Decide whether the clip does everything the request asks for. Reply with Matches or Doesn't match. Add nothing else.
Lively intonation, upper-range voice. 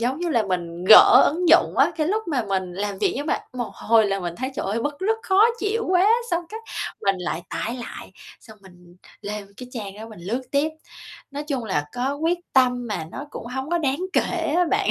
Matches